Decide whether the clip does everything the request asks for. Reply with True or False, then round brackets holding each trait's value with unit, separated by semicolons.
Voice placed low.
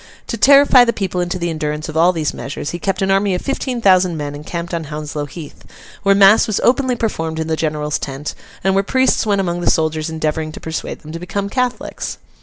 False (175 Hz)